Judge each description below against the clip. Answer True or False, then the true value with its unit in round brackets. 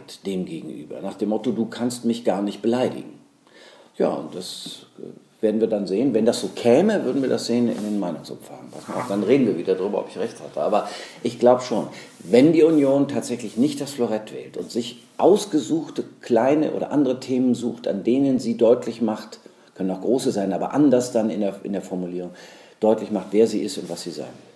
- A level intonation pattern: False (3.5 semitones)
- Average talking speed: False (205 wpm)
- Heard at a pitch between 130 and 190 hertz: False (115 Hz)